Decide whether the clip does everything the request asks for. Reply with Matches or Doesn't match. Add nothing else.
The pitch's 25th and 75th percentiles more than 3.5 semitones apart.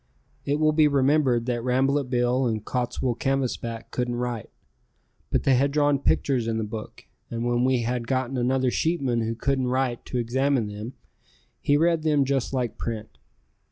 Doesn't match